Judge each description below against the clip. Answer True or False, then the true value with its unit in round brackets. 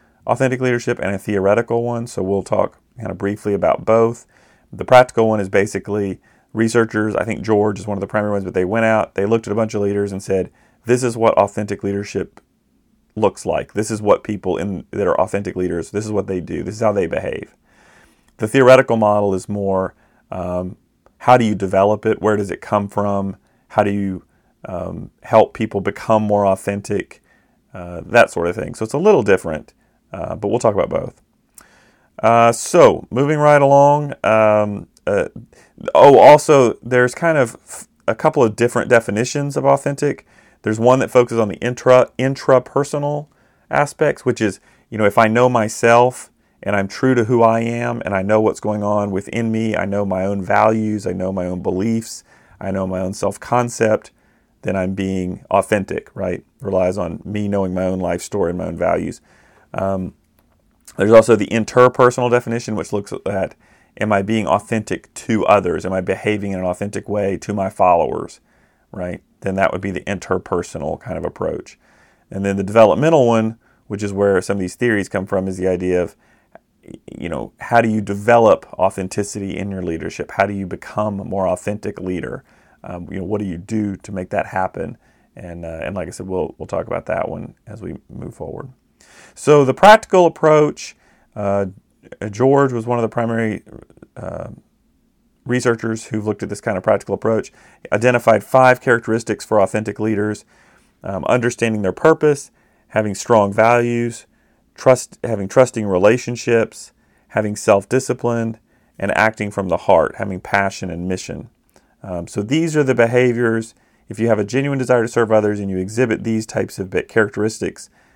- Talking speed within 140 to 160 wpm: False (185 wpm)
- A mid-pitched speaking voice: False (105 Hz)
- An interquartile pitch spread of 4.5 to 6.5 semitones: False (3.2 semitones)